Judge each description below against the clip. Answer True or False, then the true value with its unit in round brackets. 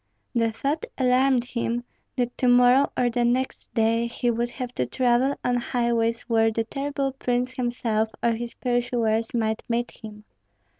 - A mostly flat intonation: True (1.5 semitones)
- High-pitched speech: True (240 Hz)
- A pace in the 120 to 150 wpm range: False (160 wpm)